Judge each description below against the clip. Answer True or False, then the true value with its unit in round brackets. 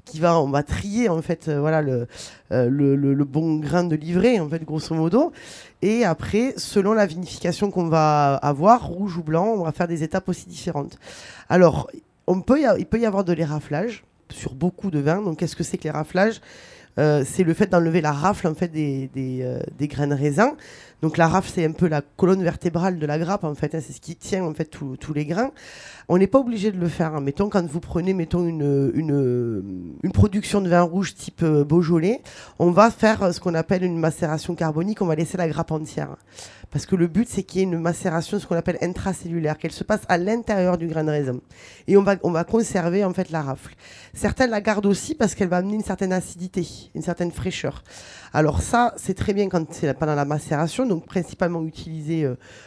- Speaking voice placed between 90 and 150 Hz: False (170 Hz)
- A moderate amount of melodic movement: True (4.0 semitones)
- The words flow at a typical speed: False (225 wpm)